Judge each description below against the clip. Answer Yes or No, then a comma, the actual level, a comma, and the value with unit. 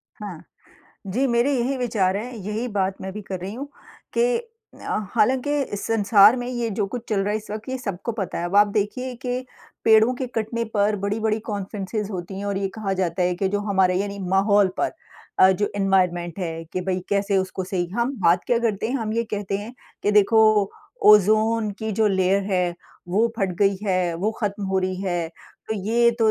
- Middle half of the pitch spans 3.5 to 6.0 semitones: No, average, 2.9 semitones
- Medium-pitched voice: No, high, 205 Hz